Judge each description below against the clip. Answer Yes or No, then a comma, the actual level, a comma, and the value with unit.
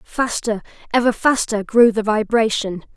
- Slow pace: Yes, slow, 120 wpm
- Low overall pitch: No, high, 225 Hz